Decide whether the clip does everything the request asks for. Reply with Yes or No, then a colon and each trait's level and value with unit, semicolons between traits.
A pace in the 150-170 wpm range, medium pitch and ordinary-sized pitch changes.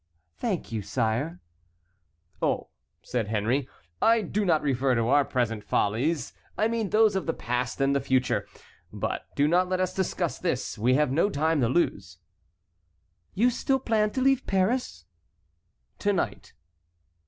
No: average, 155 wpm; medium, 145 Hz; wide, 8.1 semitones